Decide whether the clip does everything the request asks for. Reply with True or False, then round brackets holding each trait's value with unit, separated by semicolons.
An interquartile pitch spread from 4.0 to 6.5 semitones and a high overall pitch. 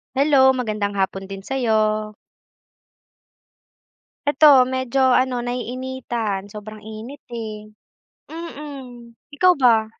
False (3.6 semitones; 240 Hz)